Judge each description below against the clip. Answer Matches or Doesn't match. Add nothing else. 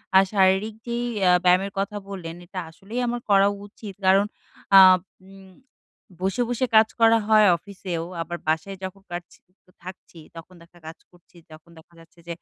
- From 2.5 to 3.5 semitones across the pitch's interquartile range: Matches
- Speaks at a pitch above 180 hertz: Matches